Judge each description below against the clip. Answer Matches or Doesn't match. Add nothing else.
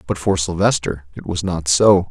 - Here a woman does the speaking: Doesn't match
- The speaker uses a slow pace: Doesn't match